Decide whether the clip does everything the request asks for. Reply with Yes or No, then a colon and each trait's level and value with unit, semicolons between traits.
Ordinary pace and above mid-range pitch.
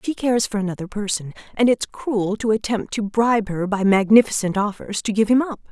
No: fast, 210 wpm; high, 215 Hz